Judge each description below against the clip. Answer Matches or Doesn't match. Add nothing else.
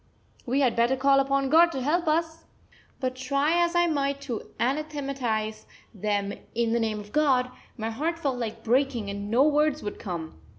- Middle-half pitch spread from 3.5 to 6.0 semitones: Matches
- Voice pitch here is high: Matches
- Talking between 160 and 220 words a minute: Matches